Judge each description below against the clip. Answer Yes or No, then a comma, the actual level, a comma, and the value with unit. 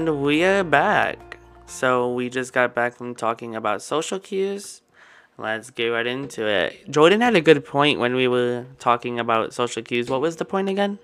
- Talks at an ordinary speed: Yes, average, 195 wpm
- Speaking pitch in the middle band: No, low, 125 Hz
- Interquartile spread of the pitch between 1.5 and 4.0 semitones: No, average, 5.2 semitones